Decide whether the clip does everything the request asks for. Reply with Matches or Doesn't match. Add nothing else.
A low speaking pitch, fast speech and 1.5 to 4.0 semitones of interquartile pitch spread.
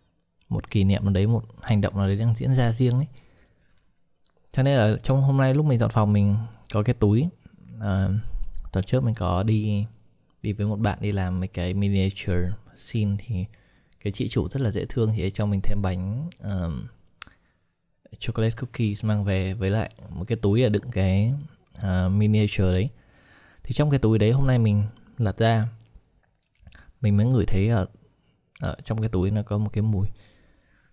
Doesn't match